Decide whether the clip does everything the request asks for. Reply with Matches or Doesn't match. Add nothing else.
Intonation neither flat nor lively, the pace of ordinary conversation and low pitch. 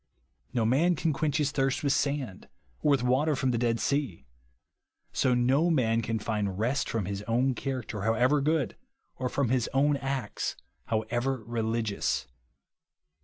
Matches